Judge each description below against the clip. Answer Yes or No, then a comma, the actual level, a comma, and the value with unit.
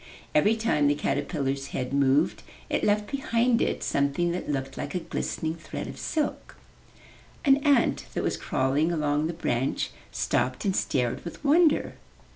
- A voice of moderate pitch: Yes, medium, 155 Hz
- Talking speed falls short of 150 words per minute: No, average, 155 wpm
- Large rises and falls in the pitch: Yes, wide, 7.8 semitones